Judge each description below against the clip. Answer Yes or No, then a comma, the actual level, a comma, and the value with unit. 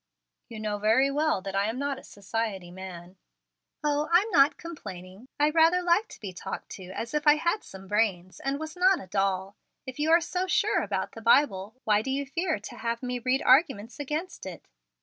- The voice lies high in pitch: Yes, very high, 255 Hz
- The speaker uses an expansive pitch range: Yes, wide, 7.3 semitones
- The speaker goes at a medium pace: No, fast, 210 wpm